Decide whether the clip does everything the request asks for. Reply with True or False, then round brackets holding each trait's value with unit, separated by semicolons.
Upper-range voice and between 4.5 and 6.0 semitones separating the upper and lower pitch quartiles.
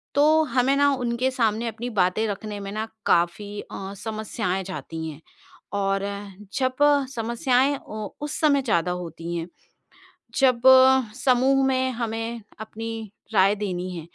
True (220 Hz; 4.8 semitones)